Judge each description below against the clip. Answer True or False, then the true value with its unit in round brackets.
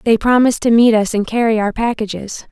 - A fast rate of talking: True (215 wpm)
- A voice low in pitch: False (225 Hz)